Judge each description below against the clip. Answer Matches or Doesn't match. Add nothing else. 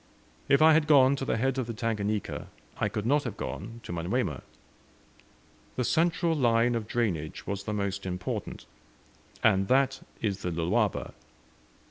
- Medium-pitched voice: Doesn't match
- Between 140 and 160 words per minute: Matches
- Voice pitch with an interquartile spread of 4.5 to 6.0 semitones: Matches